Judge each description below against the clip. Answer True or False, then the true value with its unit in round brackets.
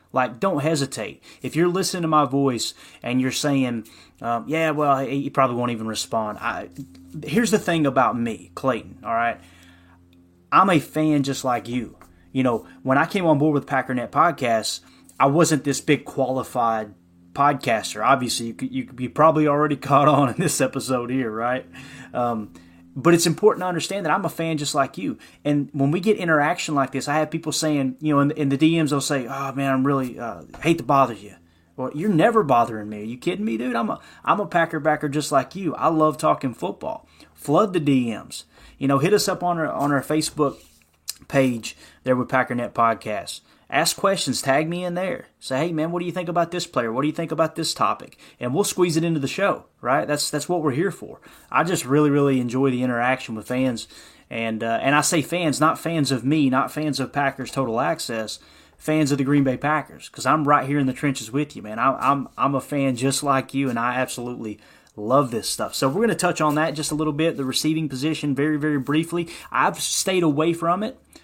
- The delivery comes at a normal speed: False (220 wpm)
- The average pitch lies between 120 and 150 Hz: True (140 Hz)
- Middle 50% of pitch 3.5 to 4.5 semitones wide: True (3.8 semitones)